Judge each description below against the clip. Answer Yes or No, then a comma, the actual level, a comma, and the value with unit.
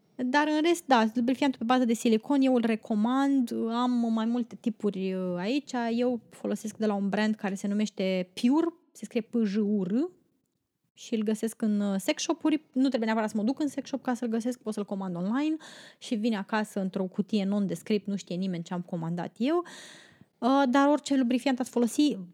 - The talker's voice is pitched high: Yes, high, 230 Hz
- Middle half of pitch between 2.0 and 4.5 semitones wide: Yes, average, 4.2 semitones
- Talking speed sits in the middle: No, fast, 195 wpm